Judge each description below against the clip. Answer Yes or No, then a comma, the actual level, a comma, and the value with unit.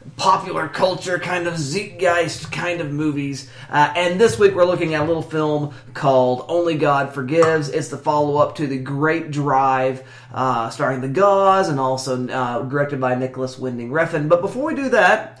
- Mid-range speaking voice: Yes, medium, 150 Hz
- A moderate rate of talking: Yes, average, 180 wpm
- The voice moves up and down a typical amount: Yes, average, 4.6 semitones